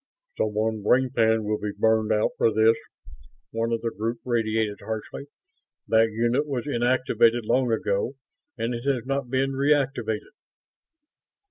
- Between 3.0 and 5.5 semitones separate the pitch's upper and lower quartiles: No, narrow, 2.5 semitones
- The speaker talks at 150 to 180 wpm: No, average, 140 wpm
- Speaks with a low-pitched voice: Yes, low, 115 Hz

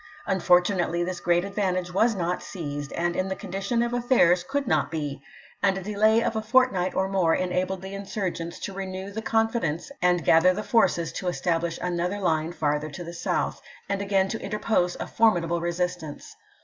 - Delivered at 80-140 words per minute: No, average, 185 wpm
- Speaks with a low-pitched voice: No, medium, 185 Hz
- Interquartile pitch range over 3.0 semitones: No, average, 2.7 semitones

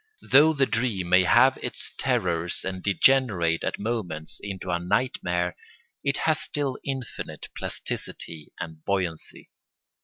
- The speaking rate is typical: No, slow, 125 wpm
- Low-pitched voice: Yes, very low, 95 Hz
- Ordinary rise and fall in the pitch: No, wide, 6.8 semitones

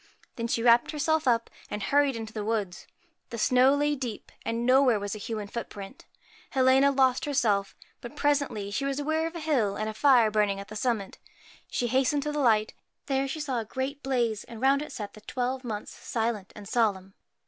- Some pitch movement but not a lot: Yes, average, 4.3 semitones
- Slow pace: No, fast, 205 wpm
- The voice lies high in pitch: Yes, high, 240 Hz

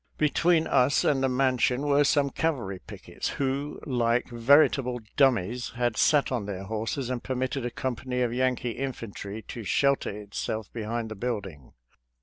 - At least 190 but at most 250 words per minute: No, average, 150 wpm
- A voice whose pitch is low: Yes, low, 125 Hz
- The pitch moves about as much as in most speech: Yes, average, 3.4 semitones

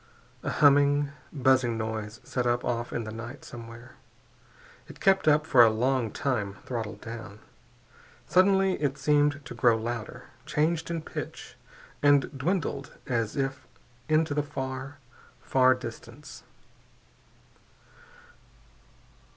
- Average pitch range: Yes, average, 3.7 semitones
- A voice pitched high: No, low, 130 Hz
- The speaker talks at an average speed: No, slow, 120 wpm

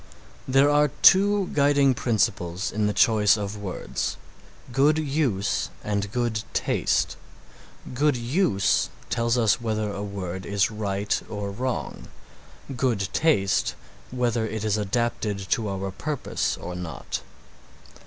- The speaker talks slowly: Yes, slow, 125 wpm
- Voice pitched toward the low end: Yes, low, 110 Hz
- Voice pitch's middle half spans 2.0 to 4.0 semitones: No, average, 4.4 semitones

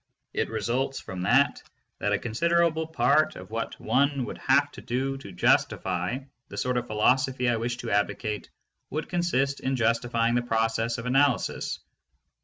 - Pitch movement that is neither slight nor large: Yes, average, 3.2 semitones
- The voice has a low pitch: Yes, low, 120 Hz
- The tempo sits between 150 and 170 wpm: Yes, average, 160 wpm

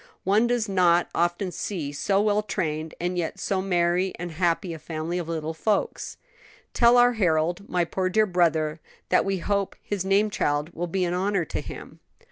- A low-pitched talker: No, medium, 180 Hz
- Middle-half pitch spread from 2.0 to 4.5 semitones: Yes, average, 3.0 semitones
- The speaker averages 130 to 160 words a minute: No, average, 185 wpm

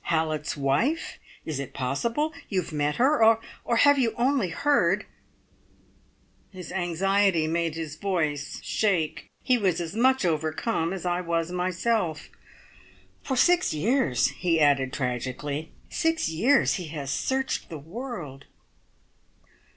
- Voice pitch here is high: No, medium, 175 Hz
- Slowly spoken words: Yes, slow, 130 wpm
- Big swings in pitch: Yes, wide, 7.1 semitones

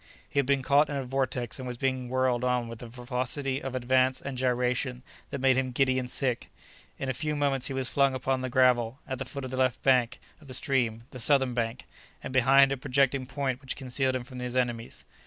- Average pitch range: No, narrow, 1.4 semitones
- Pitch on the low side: Yes, low, 130 Hz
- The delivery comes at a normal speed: No, fast, 220 wpm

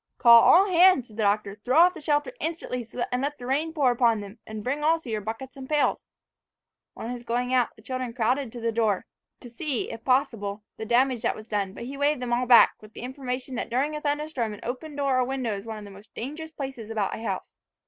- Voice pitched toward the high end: Yes, very high, 250 Hz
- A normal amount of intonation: Yes, average, 3.9 semitones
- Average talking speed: No, fast, 245 wpm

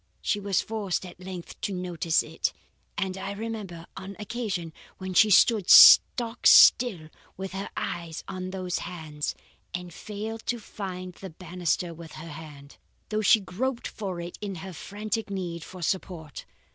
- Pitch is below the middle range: No, medium, 185 Hz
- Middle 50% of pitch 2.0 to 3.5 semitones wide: Yes, average, 3.2 semitones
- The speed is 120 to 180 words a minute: Yes, average, 160 wpm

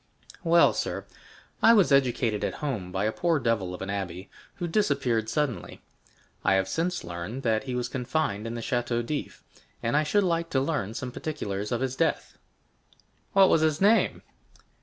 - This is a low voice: Yes, low, 125 Hz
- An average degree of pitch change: No, wide, 6.7 semitones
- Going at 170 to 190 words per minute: Yes, average, 180 wpm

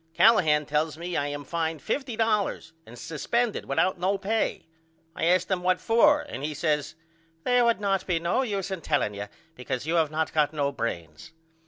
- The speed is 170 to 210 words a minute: Yes, average, 185 wpm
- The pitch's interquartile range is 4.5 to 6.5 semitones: Yes, average, 5.3 semitones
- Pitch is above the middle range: No, medium, 165 Hz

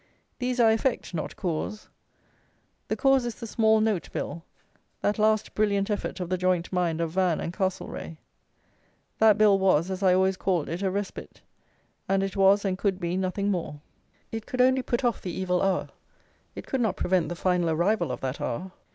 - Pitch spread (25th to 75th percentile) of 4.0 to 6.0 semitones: No, average, 3.2 semitones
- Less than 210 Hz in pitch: Yes, high, 190 Hz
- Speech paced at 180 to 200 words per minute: Yes, average, 190 wpm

